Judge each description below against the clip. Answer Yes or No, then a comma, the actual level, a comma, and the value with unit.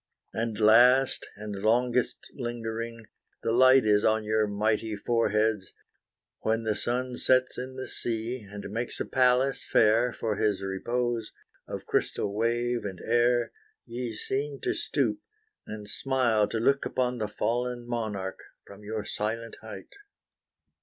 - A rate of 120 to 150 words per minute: Yes, average, 140 wpm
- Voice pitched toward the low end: Yes, low, 115 Hz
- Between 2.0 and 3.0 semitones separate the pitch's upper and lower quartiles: Yes, narrow, 2.5 semitones